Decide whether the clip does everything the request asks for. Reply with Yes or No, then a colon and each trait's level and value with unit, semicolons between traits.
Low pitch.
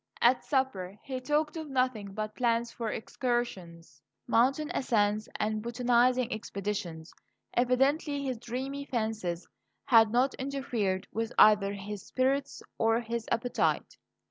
No: high, 235 Hz